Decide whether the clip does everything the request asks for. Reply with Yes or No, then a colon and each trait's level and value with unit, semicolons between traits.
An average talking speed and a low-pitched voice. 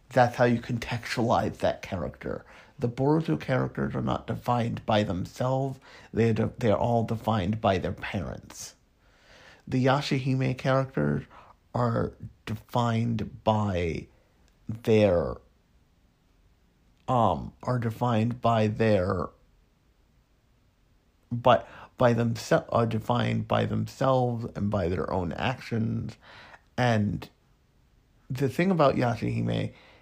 No: slow, 100 wpm; low, 115 Hz